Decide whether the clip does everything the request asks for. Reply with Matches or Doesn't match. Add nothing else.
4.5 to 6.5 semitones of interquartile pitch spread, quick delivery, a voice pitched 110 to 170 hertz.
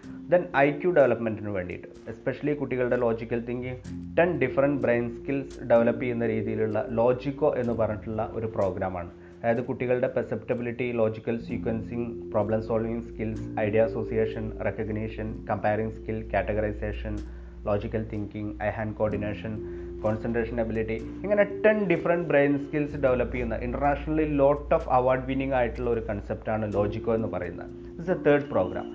Doesn't match